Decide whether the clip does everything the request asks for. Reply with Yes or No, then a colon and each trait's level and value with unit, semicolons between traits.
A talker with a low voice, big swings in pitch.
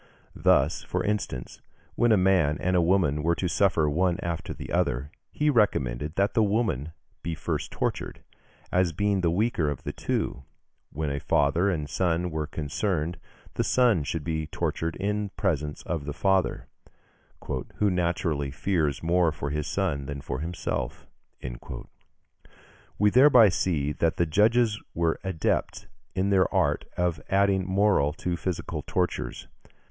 No: very low, 85 Hz; average, 4.4 semitones